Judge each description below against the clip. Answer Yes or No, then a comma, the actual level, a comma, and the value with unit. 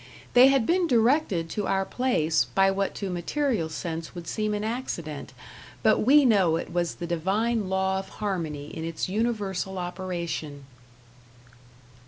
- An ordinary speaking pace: Yes, average, 150 wpm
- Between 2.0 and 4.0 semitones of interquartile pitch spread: No, average, 4.8 semitones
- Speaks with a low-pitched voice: No, high, 190 Hz